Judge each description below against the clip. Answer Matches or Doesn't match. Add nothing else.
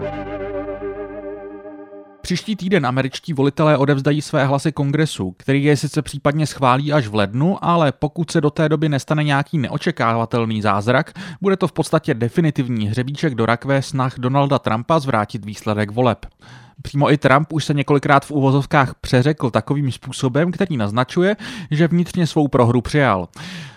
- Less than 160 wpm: Matches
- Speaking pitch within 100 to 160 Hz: Matches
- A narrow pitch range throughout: Doesn't match